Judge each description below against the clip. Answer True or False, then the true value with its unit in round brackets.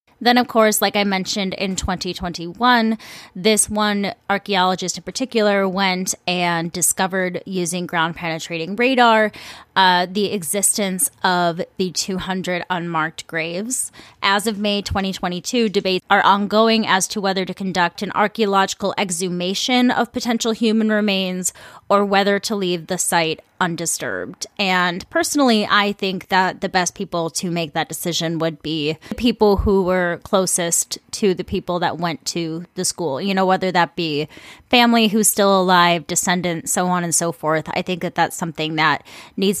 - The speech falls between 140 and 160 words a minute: True (155 wpm)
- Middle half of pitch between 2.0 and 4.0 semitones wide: True (2.8 semitones)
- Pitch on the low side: False (190 Hz)